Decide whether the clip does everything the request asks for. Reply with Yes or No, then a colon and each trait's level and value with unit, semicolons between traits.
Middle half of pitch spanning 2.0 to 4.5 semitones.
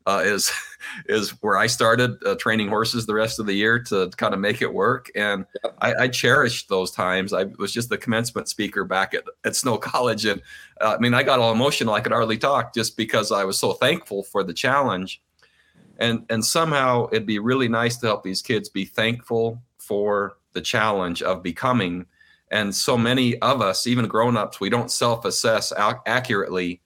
Yes: average, 3.1 semitones